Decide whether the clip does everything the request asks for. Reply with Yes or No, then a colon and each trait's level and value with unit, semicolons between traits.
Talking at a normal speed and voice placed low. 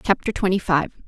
No: average, 165 wpm; medium, 185 Hz